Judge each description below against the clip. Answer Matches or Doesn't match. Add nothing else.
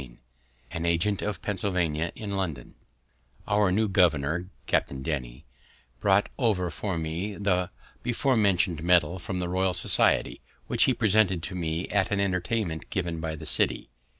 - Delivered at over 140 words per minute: Matches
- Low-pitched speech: Matches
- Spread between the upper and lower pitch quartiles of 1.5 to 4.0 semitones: Matches